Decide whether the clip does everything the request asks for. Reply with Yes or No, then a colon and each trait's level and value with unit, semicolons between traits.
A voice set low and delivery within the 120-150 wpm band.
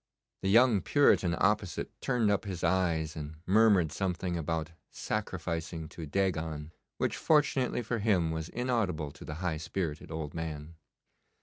Yes: very low, 85 Hz; average, 140 wpm